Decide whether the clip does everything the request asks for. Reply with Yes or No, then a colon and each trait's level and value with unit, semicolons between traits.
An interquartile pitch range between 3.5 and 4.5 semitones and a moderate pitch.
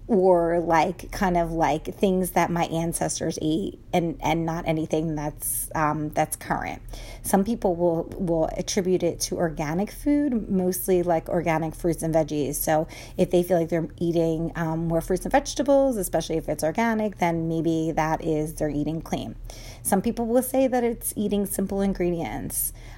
No: average, 3.0 semitones; medium, 170 Hz